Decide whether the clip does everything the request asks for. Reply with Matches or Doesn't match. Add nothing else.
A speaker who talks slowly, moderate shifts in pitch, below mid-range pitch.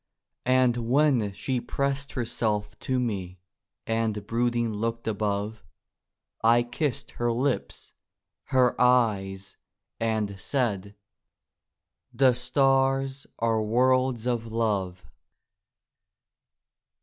Matches